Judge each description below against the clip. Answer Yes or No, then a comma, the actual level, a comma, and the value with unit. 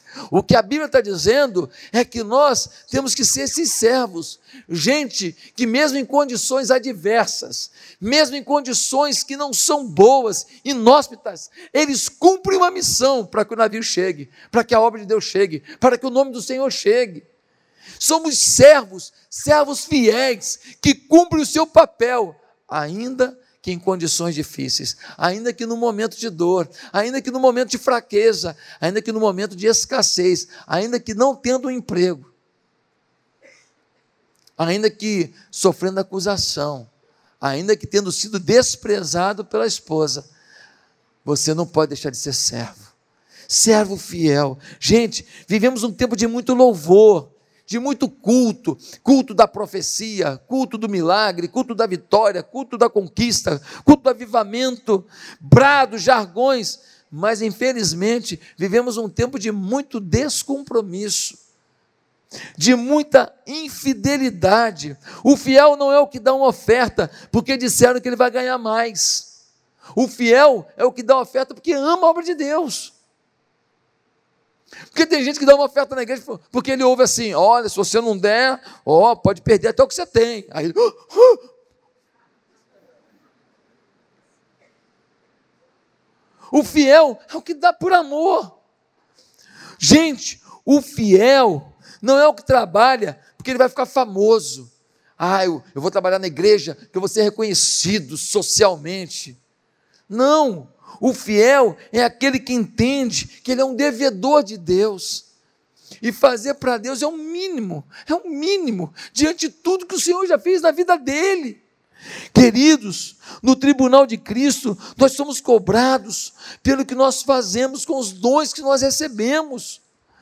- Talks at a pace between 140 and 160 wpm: Yes, average, 150 wpm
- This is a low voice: No, high, 240 Hz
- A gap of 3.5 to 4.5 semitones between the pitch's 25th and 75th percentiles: No, wide, 5.4 semitones